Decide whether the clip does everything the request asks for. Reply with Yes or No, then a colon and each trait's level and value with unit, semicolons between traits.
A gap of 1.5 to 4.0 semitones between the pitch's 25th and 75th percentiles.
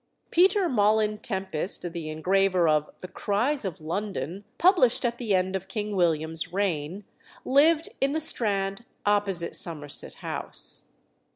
No: average, 5.1 semitones